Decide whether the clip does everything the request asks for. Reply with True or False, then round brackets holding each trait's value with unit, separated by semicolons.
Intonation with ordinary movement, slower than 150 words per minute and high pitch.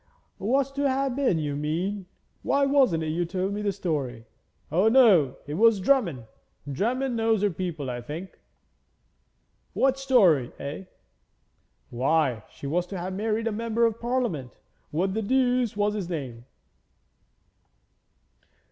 False (7.1 semitones; 140 wpm; 195 Hz)